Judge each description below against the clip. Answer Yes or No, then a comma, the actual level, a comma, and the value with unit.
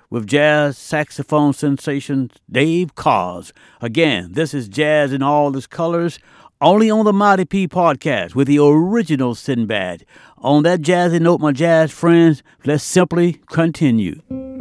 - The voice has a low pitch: No, medium, 150 Hz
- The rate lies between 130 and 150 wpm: Yes, average, 140 wpm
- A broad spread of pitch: No, average, 3.3 semitones